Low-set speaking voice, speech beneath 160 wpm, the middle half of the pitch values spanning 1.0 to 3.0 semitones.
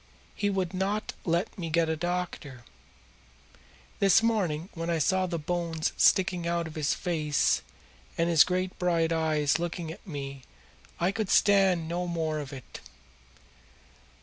No: medium, 170 Hz; average, 150 wpm; narrow, 2.5 semitones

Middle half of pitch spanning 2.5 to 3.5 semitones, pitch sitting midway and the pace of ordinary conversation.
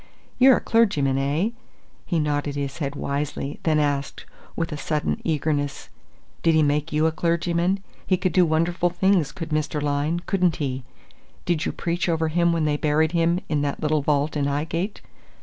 Yes: average, 2.9 semitones; medium, 155 Hz; average, 180 wpm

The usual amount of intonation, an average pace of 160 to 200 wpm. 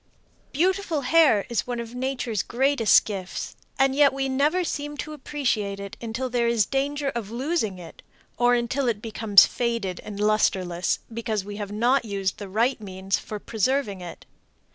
Yes: average, 4.8 semitones; average, 165 wpm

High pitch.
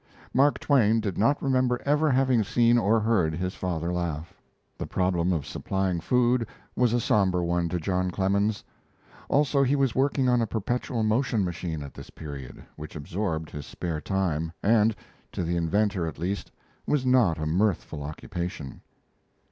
No: very low, 95 Hz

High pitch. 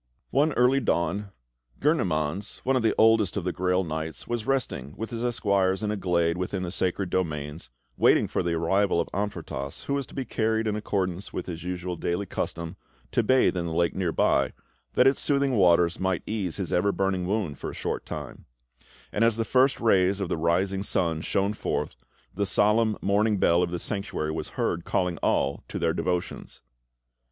No: very low, 95 Hz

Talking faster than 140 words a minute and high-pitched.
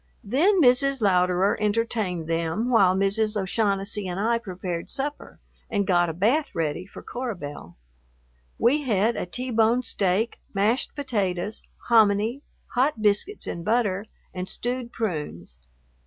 No: slow, 135 wpm; high, 210 Hz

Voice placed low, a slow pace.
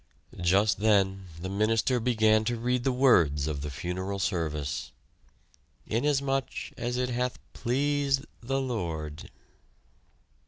Yes: low, 110 Hz; slow, 115 wpm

